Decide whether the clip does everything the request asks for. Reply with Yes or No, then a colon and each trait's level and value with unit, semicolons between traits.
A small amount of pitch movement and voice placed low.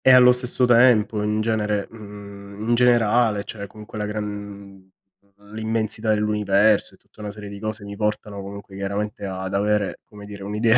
Yes: narrow, 1.5 semitones; low, 105 Hz